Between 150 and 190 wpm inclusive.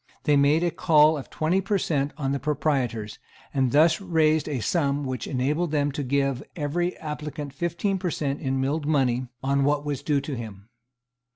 Yes: average, 185 wpm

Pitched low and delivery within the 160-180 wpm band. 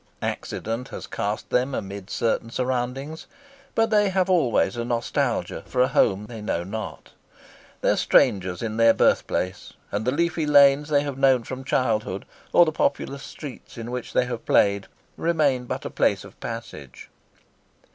Yes: low, 125 Hz; average, 165 wpm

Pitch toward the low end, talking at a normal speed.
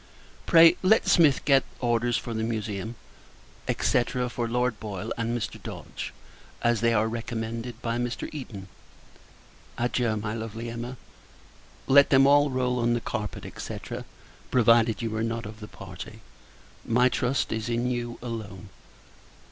Yes: low, 115 Hz; average, 145 wpm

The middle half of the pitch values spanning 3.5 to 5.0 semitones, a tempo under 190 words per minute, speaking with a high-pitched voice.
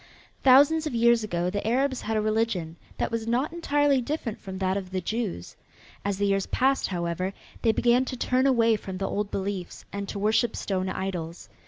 No: average, 4.4 semitones; average, 195 wpm; high, 215 Hz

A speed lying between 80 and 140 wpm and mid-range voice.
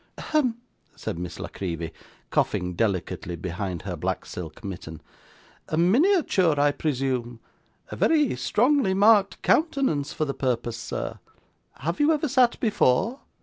Yes: slow, 135 wpm; medium, 145 Hz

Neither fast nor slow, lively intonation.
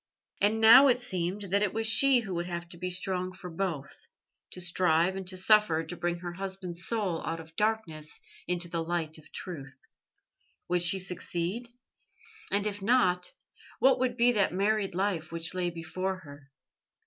No: average, 175 wpm; average, 3.3 semitones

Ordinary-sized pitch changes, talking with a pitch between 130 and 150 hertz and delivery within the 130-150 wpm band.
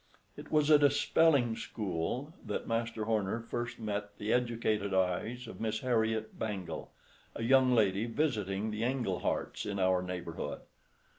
No: average, 3.3 semitones; low, 110 Hz; average, 145 wpm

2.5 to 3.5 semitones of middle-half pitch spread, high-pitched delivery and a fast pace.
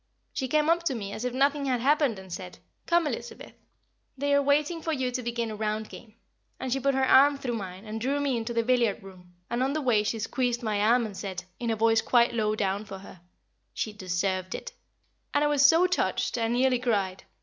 No: average, 4.5 semitones; high, 235 Hz; fast, 230 wpm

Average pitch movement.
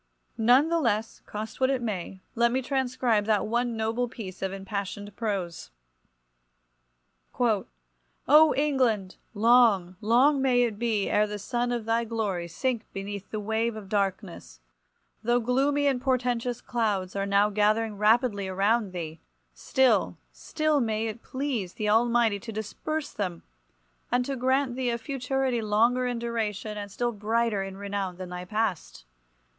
Yes: average, 3.5 semitones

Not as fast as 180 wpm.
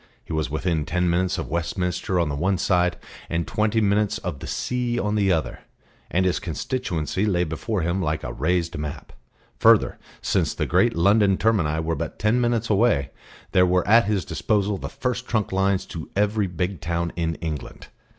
No: average, 185 wpm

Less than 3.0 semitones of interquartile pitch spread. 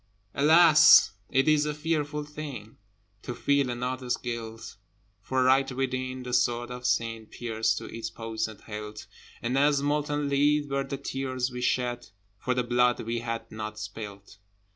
No: average, 3.6 semitones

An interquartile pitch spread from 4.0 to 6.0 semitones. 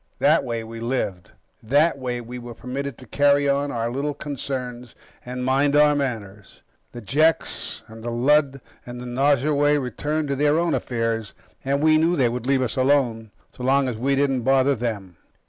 No: average, 3.1 semitones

